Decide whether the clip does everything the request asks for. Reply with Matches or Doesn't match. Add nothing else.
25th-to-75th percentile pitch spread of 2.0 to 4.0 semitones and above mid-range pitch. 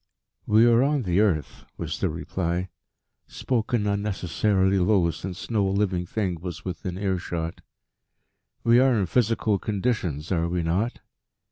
Doesn't match